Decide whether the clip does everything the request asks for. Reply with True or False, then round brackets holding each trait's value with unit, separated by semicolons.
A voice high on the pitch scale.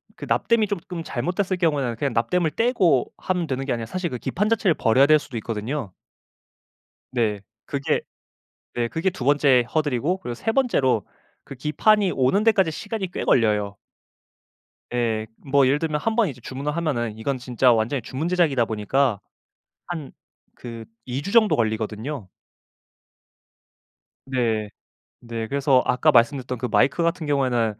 False (135 Hz)